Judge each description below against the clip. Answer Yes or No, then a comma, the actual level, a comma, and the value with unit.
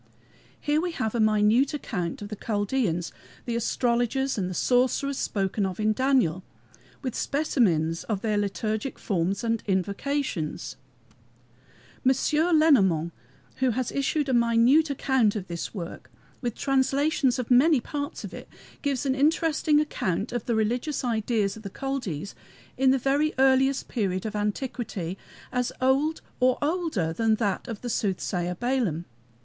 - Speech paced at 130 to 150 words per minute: Yes, average, 145 wpm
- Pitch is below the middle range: No, high, 235 Hz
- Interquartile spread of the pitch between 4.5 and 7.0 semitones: Yes, average, 5.1 semitones